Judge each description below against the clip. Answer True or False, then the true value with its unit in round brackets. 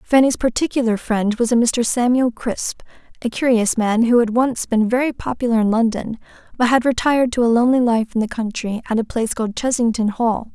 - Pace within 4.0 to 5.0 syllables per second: False (5.6 syllables/s)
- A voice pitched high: True (235 Hz)